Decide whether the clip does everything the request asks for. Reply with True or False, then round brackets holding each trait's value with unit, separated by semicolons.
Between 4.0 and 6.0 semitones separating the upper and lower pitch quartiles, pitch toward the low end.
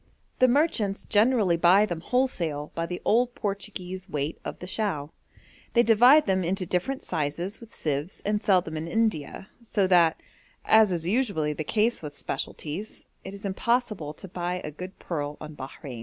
False (5.2 semitones; 185 Hz)